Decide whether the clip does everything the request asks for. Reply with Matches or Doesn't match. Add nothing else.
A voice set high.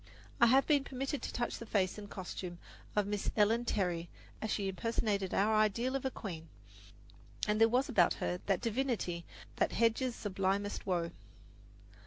Matches